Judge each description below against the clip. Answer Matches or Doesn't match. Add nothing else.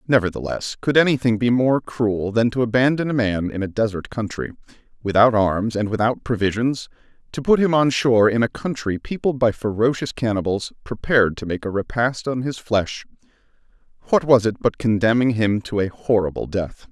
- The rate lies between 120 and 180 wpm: Matches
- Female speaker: Doesn't match